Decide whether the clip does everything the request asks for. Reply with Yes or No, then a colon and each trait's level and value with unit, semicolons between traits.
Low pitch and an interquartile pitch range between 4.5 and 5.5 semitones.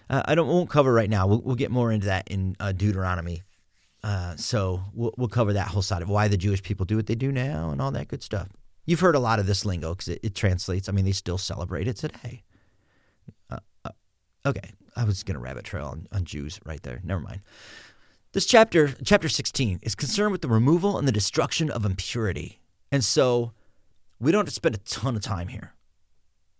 Yes: low, 105 Hz; average, 5.1 semitones